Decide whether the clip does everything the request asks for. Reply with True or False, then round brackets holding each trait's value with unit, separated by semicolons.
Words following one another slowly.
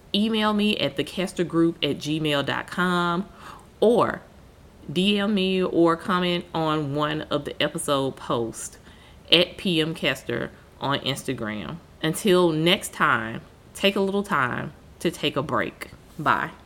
True (120 wpm)